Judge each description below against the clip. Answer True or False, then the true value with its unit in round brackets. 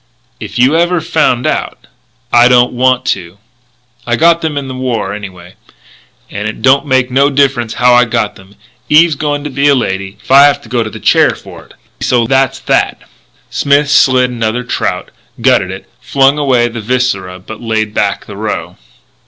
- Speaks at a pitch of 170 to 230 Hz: False (125 Hz)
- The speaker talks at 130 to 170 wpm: False (185 wpm)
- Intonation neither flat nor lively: True (3.7 semitones)